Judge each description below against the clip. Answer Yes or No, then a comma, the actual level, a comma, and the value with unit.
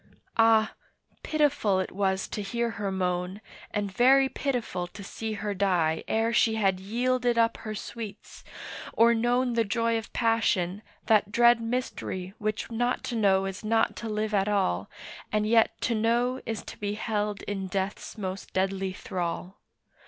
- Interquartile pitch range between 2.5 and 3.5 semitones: Yes, average, 3.2 semitones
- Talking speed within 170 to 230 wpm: No, average, 160 wpm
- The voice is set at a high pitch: Yes, high, 215 Hz